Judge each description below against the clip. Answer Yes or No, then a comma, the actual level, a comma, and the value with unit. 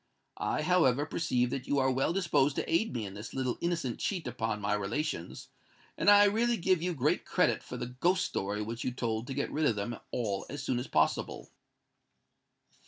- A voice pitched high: No, low, 130 Hz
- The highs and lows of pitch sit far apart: Yes, wide, 6.7 semitones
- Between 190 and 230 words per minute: Yes, average, 200 wpm